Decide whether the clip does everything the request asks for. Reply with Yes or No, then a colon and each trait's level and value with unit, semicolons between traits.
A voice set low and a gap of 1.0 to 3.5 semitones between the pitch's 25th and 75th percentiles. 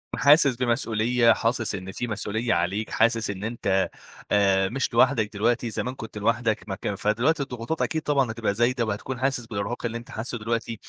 Yes: low, 115 Hz; average, 2.7 semitones